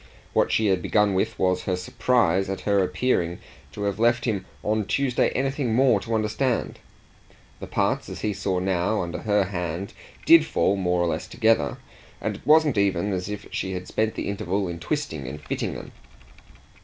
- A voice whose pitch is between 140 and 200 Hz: No, low, 100 Hz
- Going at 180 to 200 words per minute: Yes, average, 185 wpm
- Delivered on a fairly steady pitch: No, average, 3.8 semitones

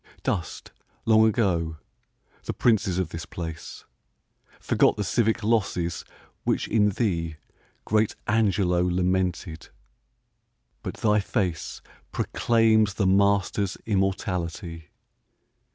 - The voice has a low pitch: Yes, very low, 95 Hz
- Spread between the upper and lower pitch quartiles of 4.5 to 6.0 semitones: No, average, 3.6 semitones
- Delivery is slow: Yes, slow, 95 wpm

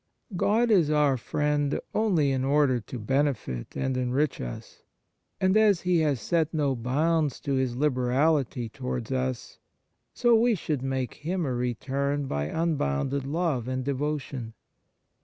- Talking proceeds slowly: No, average, 145 wpm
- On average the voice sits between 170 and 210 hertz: No, medium, 140 Hz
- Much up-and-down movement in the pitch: No, average, 3.7 semitones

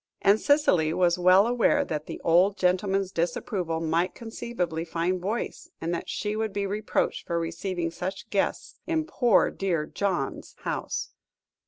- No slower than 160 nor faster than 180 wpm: No, average, 150 wpm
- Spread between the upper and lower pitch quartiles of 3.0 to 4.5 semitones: Yes, average, 3.4 semitones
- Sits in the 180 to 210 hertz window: Yes, medium, 185 Hz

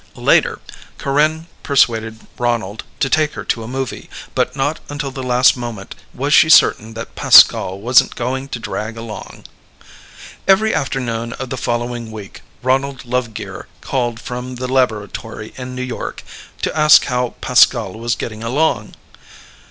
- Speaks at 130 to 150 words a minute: Yes, average, 145 wpm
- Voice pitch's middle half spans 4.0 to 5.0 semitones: No, average, 2.8 semitones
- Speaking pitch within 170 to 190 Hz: No, low, 125 Hz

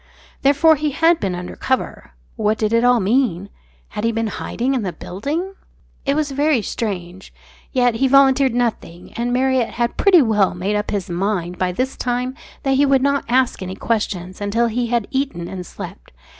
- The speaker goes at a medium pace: Yes, average, 185 wpm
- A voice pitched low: No, high, 235 Hz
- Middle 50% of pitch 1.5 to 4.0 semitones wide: No, average, 5.2 semitones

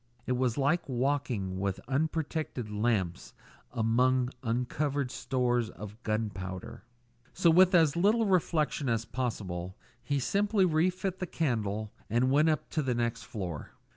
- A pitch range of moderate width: No, wide, 6.2 semitones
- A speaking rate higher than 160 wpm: No, average, 140 wpm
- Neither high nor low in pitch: No, low, 125 Hz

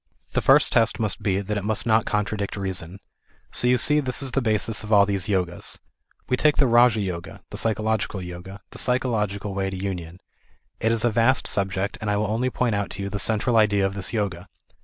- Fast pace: Yes, fast, 220 wpm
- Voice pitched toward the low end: Yes, low, 105 Hz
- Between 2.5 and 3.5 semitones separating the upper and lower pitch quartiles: Yes, average, 2.8 semitones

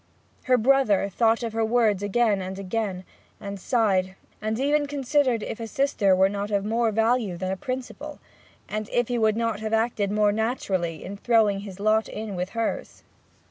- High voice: Yes, high, 215 Hz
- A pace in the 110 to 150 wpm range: No, average, 180 wpm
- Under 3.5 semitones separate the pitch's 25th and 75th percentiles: Yes, average, 3.0 semitones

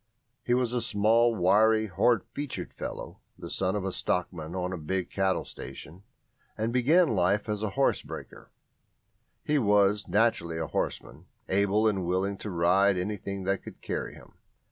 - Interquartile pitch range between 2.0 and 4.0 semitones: Yes, average, 3.1 semitones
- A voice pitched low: Yes, low, 100 Hz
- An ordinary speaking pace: Yes, average, 165 wpm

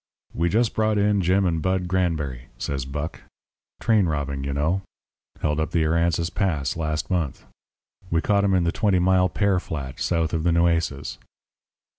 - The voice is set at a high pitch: No, very low, 85 Hz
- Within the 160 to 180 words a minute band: Yes, average, 170 wpm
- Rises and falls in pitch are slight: No, average, 3.4 semitones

